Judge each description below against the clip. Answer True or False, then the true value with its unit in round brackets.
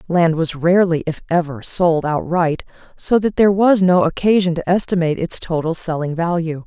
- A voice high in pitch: False (170 Hz)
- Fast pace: False (170 wpm)